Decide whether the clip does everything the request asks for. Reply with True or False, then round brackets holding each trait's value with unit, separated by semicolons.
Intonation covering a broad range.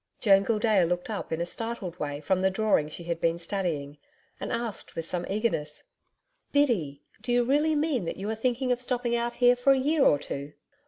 True (6.4 semitones)